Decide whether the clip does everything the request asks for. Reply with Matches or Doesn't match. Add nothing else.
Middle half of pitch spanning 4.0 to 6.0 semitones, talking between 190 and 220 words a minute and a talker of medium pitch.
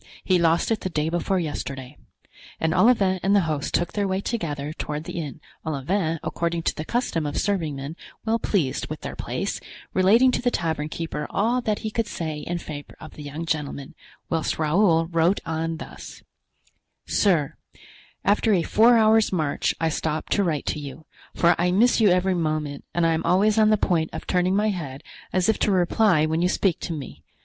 Matches